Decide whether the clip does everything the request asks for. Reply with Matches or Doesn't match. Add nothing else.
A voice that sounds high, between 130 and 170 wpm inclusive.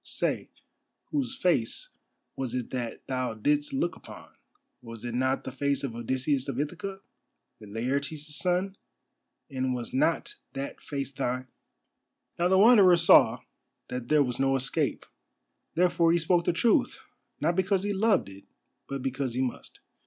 Doesn't match